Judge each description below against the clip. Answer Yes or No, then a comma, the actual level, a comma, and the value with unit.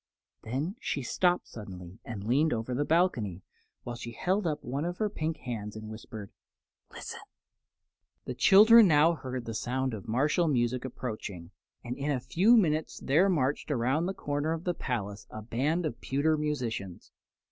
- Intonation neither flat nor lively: No, wide, 5.8 semitones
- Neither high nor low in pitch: No, low, 130 Hz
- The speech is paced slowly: No, average, 170 wpm